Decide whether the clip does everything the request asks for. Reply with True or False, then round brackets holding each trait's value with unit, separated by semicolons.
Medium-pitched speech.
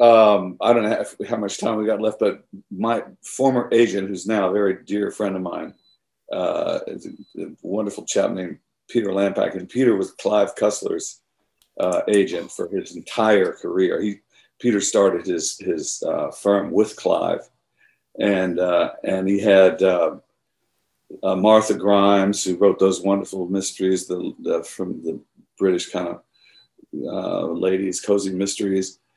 False (100 Hz)